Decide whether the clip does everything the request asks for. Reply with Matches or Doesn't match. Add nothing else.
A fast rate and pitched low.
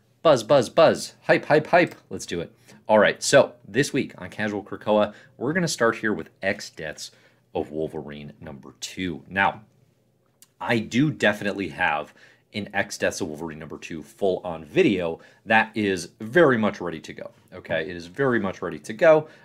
Doesn't match